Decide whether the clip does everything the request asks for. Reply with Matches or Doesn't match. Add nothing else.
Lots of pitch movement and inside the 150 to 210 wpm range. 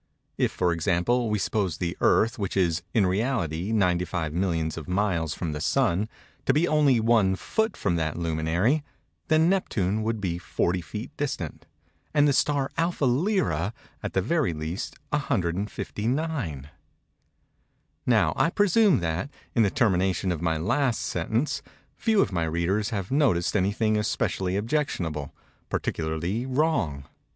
Doesn't match